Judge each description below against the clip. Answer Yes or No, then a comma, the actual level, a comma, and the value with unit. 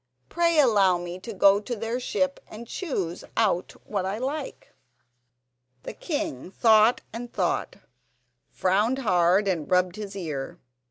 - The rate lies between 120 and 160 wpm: Yes, average, 140 wpm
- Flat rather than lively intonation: No, average, 4.8 semitones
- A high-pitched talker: Yes, high, 210 Hz